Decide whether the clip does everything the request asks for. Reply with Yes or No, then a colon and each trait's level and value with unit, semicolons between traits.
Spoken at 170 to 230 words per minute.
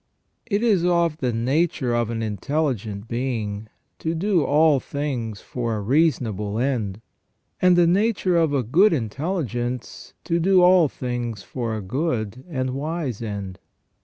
No: average, 145 wpm